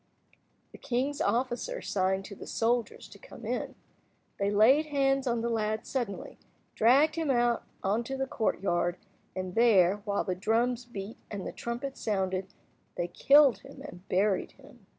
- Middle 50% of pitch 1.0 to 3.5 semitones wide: No, average, 4.7 semitones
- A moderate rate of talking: Yes, average, 155 wpm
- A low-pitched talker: No, high, 225 Hz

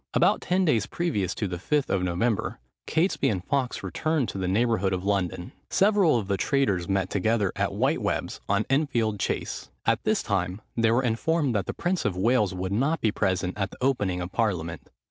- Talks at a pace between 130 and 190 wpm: No, average, 200 wpm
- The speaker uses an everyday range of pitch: No, wide, 6.4 semitones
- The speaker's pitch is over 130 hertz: No, low, 105 Hz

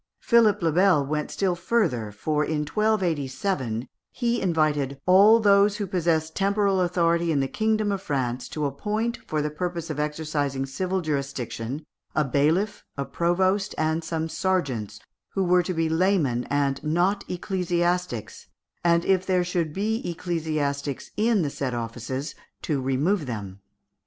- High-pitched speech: No, medium, 165 Hz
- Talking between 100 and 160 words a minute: Yes, average, 145 wpm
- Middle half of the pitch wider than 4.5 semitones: Yes, average, 5.0 semitones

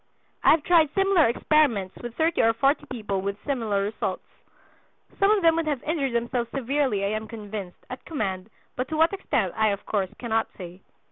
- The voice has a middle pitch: No, high, 235 Hz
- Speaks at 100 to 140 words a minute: No, average, 190 wpm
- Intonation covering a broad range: Yes, wide, 6.8 semitones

